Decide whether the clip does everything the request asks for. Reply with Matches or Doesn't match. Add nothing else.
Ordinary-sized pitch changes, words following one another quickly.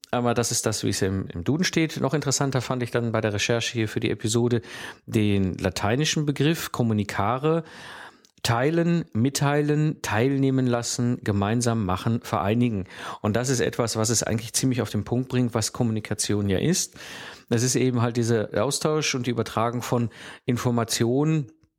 Doesn't match